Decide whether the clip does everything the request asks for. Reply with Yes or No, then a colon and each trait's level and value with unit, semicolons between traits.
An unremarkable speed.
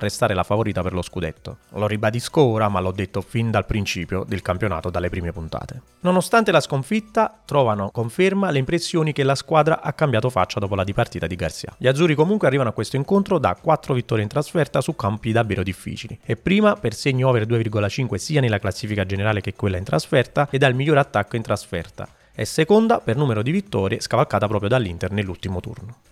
No: fast, 195 wpm